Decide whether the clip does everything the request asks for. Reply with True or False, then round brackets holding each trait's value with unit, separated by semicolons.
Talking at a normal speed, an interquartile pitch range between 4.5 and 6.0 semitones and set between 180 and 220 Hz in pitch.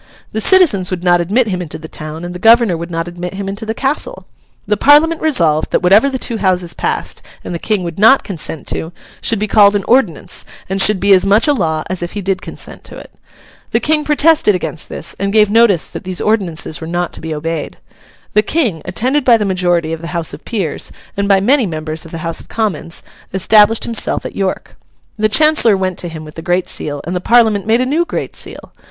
False (230 wpm; 4.8 semitones; 195 Hz)